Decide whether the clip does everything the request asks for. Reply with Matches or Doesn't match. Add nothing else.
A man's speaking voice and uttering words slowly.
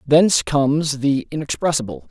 Matches